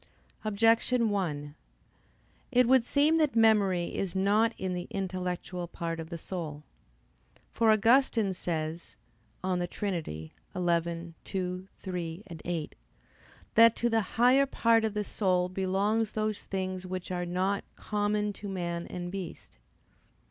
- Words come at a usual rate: No, slow, 125 wpm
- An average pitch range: Yes, average, 3.6 semitones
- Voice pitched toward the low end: No, high, 190 Hz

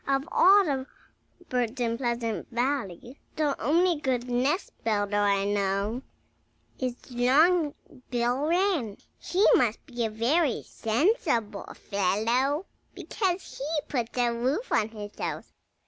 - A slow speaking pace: Yes, slow, 125 wpm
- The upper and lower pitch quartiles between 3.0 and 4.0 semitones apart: No, average, 4.8 semitones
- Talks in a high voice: Yes, high, 245 Hz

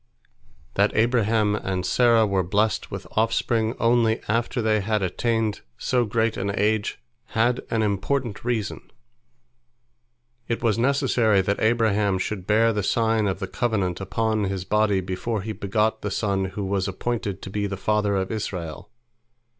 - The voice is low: Yes, low, 105 Hz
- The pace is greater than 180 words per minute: No, average, 155 wpm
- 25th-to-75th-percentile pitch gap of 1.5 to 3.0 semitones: Yes, narrow, 2.6 semitones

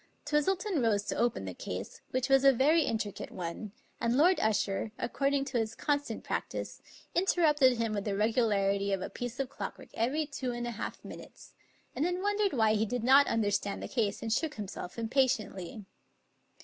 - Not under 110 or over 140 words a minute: No, average, 195 wpm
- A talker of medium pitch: No, high, 240 Hz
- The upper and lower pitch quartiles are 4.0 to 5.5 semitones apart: Yes, average, 5.2 semitones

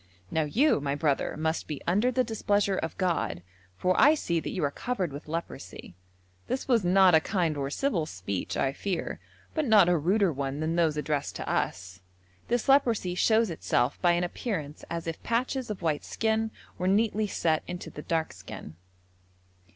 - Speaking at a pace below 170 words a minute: No, average, 180 wpm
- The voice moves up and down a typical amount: No, wide, 6.3 semitones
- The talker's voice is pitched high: No, medium, 175 Hz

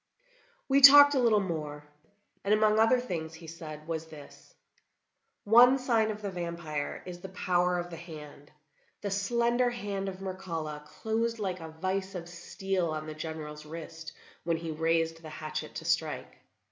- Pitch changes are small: No, average, 4.6 semitones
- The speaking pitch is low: No, medium, 175 Hz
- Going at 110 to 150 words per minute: No, average, 165 wpm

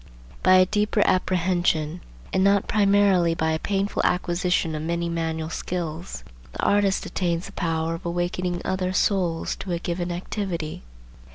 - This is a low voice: No, medium, 175 Hz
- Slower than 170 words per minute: Yes, average, 150 wpm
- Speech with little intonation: Yes, narrow, 2.2 semitones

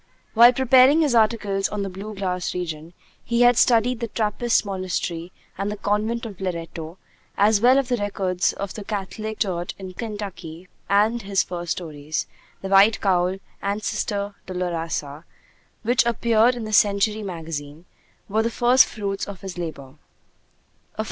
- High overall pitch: Yes, high, 200 Hz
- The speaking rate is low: No, average, 155 wpm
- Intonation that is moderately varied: Yes, average, 3.8 semitones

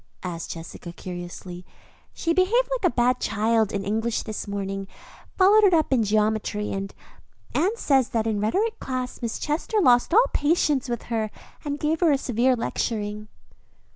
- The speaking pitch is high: Yes, high, 235 Hz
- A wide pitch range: Yes, wide, 6.7 semitones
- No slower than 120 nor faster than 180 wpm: Yes, average, 165 wpm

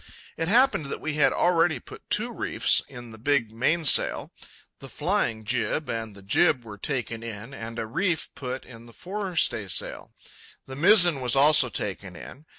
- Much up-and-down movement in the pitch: Yes, wide, 5.9 semitones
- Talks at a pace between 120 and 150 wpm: No, average, 170 wpm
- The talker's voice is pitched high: No, low, 130 Hz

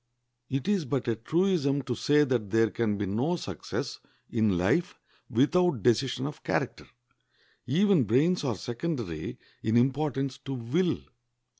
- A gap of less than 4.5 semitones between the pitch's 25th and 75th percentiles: No, average, 5.2 semitones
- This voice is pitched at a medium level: No, low, 130 Hz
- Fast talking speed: No, average, 140 wpm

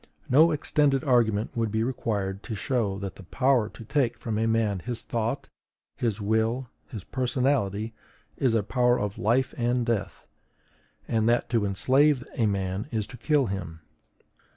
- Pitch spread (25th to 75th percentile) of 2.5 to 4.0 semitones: Yes, average, 3.5 semitones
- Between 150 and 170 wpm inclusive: Yes, average, 160 wpm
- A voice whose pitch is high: No, low, 115 Hz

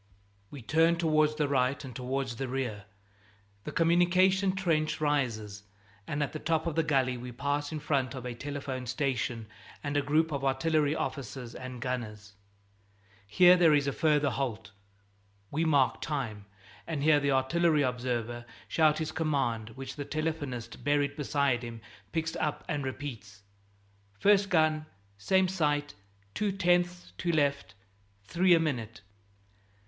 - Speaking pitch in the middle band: Yes, medium, 145 Hz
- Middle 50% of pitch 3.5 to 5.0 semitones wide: Yes, average, 3.9 semitones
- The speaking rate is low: No, average, 150 wpm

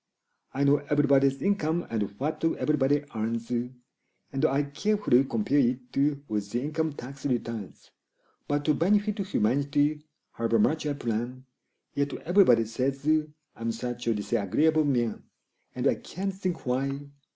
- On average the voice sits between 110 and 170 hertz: Yes, medium, 140 Hz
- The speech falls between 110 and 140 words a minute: Yes, slow, 135 wpm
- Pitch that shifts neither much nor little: Yes, average, 4.1 semitones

